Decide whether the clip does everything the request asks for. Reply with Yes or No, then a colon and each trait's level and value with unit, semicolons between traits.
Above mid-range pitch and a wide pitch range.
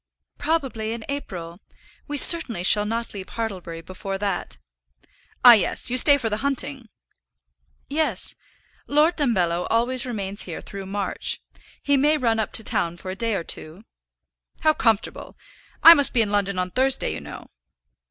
Yes: high, 225 Hz; wide, 5.8 semitones